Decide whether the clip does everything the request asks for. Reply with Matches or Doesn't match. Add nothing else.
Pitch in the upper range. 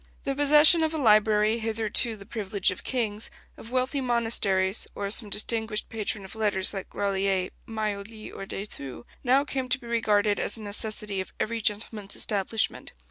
Matches